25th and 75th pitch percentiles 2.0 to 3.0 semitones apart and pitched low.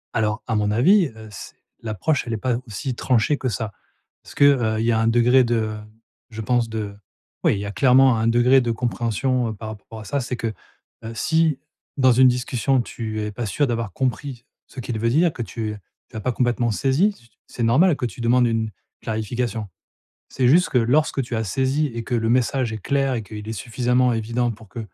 Yes: narrow, 2.6 semitones; low, 120 Hz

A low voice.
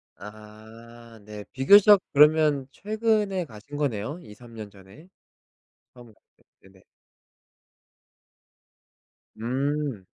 Yes: low, 120 Hz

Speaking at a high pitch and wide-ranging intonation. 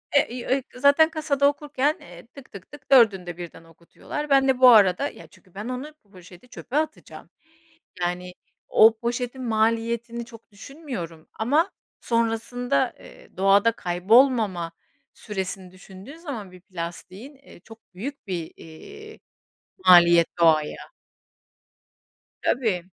Yes: high, 225 Hz; wide, 6.8 semitones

